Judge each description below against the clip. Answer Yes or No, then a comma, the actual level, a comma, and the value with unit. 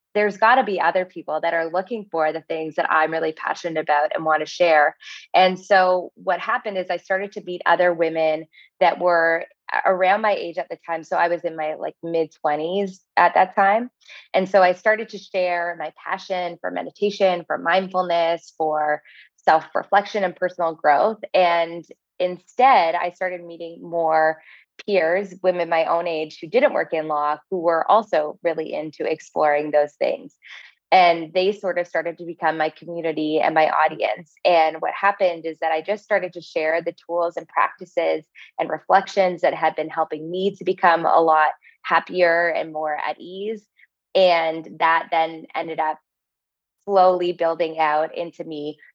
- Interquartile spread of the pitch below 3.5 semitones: Yes, average, 2.8 semitones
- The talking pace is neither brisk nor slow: Yes, average, 175 wpm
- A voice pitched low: No, medium, 170 Hz